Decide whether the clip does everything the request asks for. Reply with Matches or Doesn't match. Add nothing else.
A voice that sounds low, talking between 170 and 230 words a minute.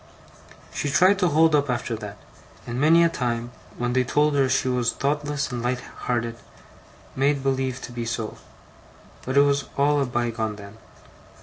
Matches